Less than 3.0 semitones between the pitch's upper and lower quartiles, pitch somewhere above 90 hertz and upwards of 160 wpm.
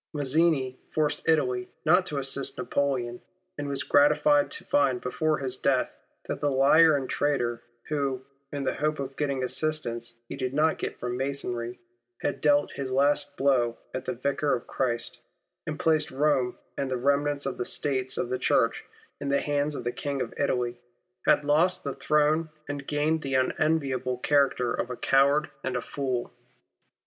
Yes: narrow, 2.4 semitones; medium, 140 Hz; average, 175 wpm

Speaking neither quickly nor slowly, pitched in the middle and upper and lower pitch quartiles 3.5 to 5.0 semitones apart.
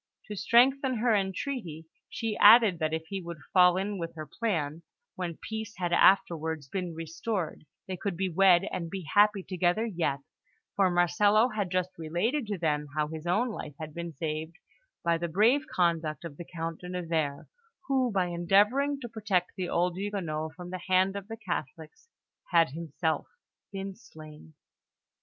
Yes: average, 170 wpm; medium, 180 Hz; average, 4.1 semitones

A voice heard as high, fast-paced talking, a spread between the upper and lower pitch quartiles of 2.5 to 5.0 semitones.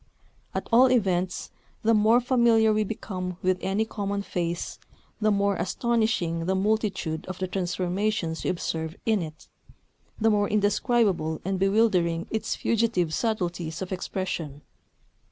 No: high, 195 Hz; slow, 135 wpm; average, 3.8 semitones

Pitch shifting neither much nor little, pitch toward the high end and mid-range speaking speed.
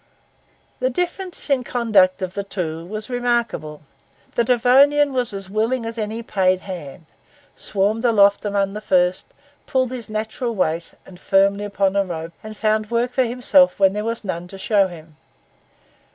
Yes: average, 4.1 semitones; high, 210 Hz; average, 165 wpm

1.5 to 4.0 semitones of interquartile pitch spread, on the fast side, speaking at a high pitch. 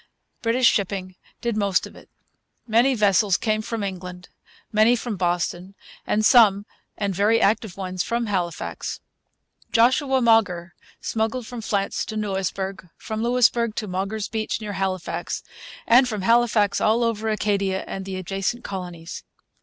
No: average, 3.2 semitones; average, 140 wpm; high, 210 Hz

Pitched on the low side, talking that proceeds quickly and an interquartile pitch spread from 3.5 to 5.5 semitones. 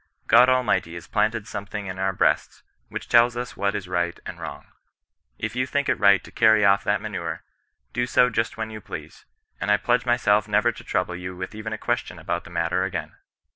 Yes: low, 105 Hz; fast, 215 wpm; average, 4.0 semitones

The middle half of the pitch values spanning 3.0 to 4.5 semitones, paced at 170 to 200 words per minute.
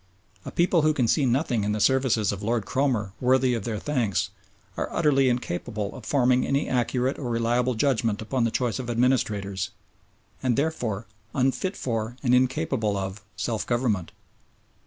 No: average, 3.3 semitones; average, 160 wpm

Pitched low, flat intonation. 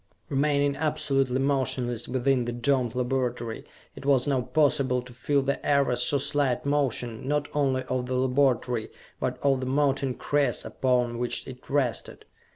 Yes: low, 130 Hz; narrow, 2.2 semitones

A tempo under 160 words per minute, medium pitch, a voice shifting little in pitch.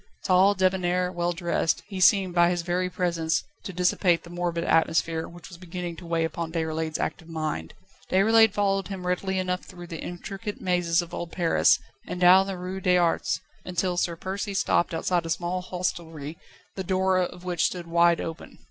No: average, 185 wpm; medium, 175 Hz; narrow, 1.8 semitones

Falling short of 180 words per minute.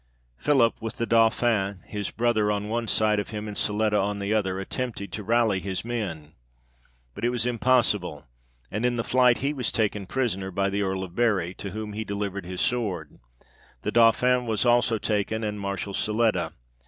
No: average, 185 wpm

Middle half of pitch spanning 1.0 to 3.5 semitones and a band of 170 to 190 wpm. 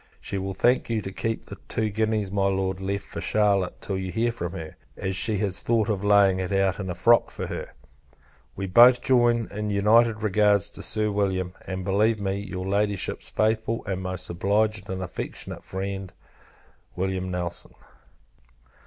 Yes: narrow, 2.4 semitones; average, 175 wpm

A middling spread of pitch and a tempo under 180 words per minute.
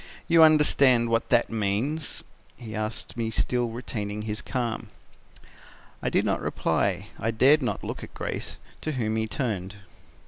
Yes: average, 3.1 semitones; average, 150 wpm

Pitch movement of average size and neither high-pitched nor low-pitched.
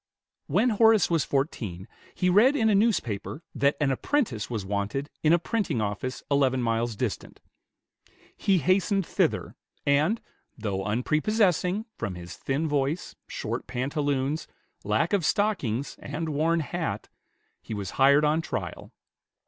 No: wide, 7.0 semitones; medium, 145 Hz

